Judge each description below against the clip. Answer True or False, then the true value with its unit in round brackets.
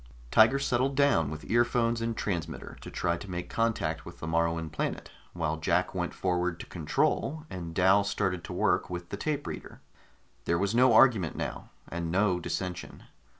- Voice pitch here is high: False (90 Hz)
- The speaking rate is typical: True (175 wpm)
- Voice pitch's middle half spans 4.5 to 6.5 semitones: True (5.2 semitones)